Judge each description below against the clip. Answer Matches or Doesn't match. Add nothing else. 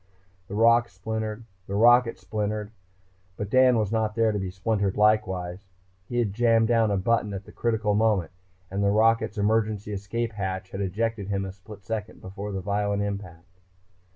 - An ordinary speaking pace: Matches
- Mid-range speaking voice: Doesn't match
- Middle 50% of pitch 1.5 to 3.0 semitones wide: Matches